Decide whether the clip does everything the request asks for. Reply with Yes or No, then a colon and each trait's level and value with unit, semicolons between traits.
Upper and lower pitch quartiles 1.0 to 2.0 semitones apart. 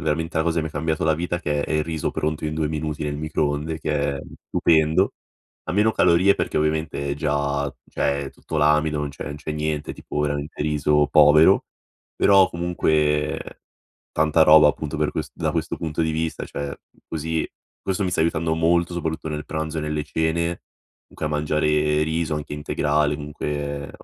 Yes: narrow, 1.3 semitones